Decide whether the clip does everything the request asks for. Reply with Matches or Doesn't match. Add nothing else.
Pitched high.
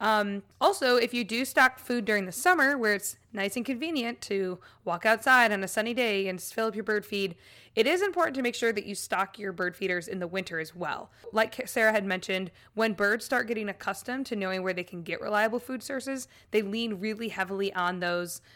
Matches